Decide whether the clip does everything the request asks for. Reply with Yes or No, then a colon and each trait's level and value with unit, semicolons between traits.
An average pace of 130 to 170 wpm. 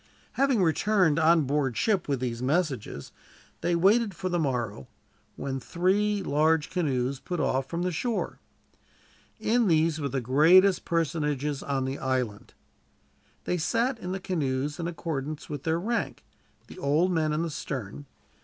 Yes: average, 155 wpm